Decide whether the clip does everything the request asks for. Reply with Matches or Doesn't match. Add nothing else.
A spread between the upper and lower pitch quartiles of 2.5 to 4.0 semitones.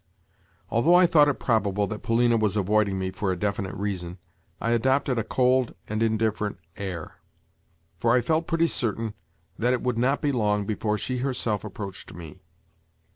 Matches